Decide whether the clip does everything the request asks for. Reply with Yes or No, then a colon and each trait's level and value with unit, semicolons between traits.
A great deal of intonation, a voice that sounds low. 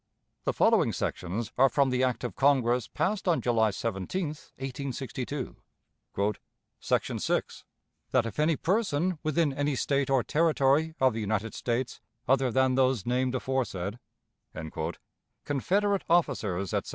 No: average, 3.8 semitones; low, 130 Hz